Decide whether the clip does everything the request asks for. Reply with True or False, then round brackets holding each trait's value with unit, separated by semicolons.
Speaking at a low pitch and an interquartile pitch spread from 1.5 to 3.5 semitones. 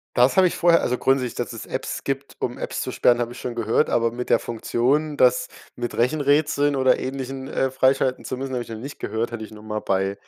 True (125 Hz; 2.5 semitones)